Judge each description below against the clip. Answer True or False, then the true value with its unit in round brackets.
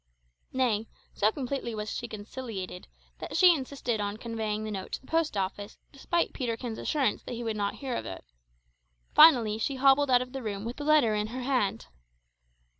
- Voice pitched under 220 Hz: False (235 Hz)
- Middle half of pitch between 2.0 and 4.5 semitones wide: True (4.1 semitones)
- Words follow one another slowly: False (190 wpm)